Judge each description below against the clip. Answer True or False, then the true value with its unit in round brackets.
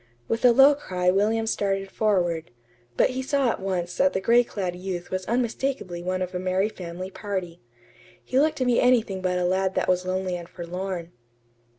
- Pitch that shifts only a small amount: False (4.2 semitones)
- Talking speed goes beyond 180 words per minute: True (195 wpm)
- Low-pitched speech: False (190 Hz)